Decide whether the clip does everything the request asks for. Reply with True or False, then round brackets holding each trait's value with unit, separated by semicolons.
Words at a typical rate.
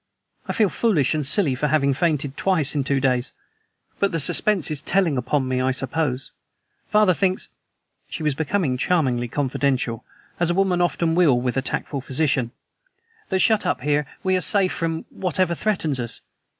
True (175 wpm)